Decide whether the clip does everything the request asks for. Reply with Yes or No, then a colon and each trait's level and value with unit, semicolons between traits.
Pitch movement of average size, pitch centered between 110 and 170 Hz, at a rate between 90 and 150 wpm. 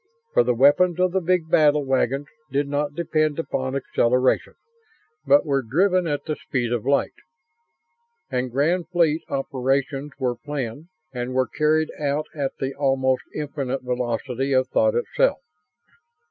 Yes: average, 3.0 semitones; medium, 140 Hz; average, 145 wpm